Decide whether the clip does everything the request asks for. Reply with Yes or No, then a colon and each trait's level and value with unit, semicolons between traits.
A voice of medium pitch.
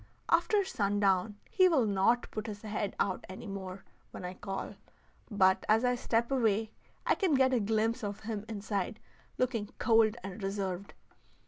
No: high, 210 Hz